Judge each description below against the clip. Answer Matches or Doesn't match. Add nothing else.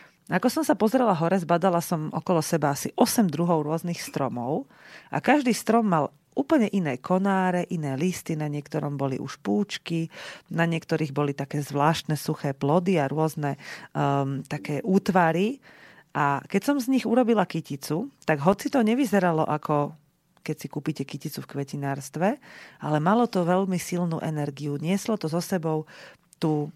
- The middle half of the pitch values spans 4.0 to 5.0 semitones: Matches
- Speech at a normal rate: Matches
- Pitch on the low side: Doesn't match